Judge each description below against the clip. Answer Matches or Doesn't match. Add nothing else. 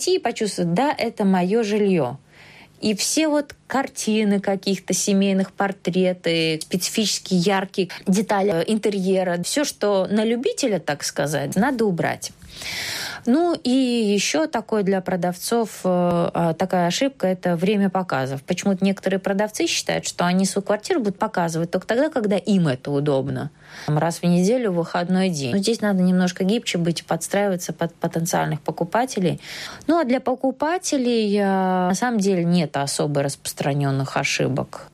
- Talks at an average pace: Matches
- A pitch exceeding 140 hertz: Matches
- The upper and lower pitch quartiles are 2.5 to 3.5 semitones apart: Doesn't match